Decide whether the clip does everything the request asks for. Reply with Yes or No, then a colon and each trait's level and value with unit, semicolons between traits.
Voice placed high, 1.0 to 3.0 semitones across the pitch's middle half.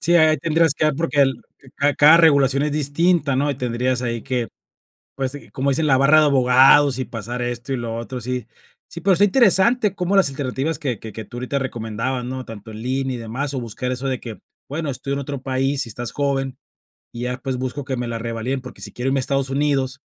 No: low, 135 Hz; narrow, 2.6 semitones